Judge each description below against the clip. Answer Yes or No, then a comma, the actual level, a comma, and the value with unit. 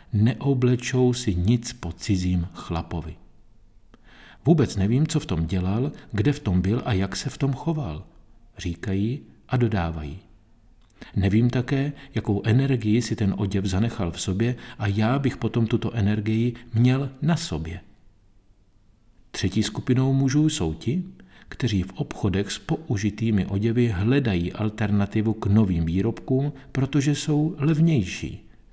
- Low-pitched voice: Yes, low, 110 Hz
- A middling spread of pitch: Yes, average, 4.6 semitones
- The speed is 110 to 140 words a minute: Yes, average, 130 wpm